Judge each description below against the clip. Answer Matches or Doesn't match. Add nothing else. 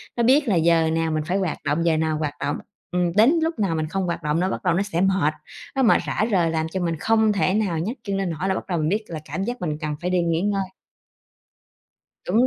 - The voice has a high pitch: Doesn't match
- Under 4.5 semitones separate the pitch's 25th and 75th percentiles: Matches